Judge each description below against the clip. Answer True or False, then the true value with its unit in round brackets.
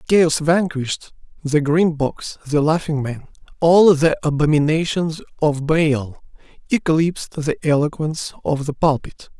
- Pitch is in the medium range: True (155 Hz)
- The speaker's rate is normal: False (120 wpm)